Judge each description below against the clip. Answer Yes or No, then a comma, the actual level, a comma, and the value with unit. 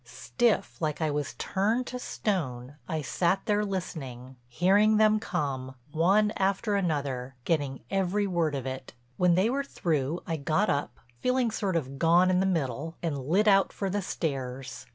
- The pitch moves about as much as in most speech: No, wide, 6.2 semitones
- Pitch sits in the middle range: Yes, medium, 170 Hz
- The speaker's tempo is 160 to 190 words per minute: Yes, average, 170 wpm